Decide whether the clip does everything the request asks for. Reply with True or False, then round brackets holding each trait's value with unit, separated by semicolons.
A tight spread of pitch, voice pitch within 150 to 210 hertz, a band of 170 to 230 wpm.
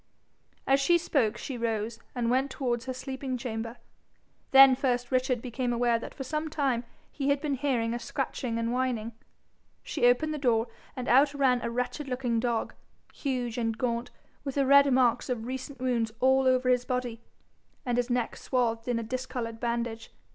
False (2.2 semitones; 250 Hz; 180 wpm)